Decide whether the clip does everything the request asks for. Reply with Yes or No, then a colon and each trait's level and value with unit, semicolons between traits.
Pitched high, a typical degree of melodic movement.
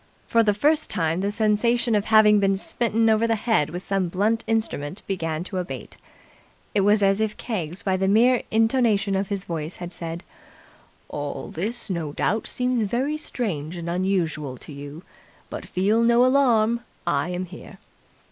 Yes: high, 200 Hz; average, 4.5 semitones